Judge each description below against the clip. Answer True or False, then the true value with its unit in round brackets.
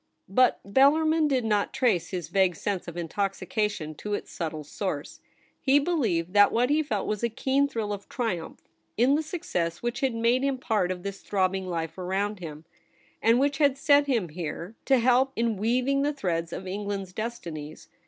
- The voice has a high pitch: True (210 Hz)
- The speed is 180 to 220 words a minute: True (185 wpm)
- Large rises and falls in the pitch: True (6.4 semitones)